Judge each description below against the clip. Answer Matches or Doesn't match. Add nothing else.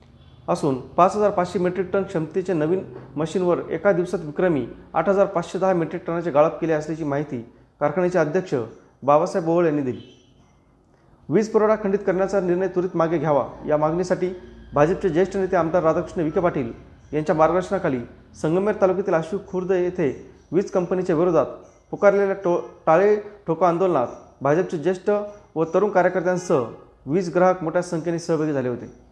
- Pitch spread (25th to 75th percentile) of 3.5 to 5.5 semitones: Doesn't match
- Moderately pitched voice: Matches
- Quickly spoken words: Matches